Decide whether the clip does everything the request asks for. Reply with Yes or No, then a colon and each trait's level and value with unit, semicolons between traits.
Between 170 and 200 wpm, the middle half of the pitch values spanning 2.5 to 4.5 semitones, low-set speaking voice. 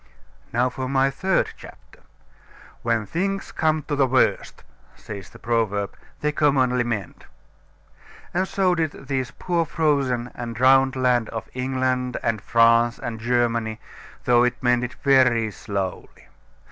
No: slow, 135 wpm; average, 2.8 semitones; low, 125 Hz